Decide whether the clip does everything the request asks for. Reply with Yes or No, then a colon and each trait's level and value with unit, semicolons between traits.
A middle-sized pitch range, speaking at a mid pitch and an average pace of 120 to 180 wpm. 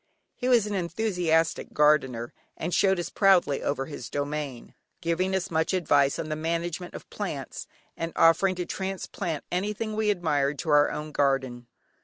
Yes: average, 4.3 semitones; medium, 165 Hz; average, 160 wpm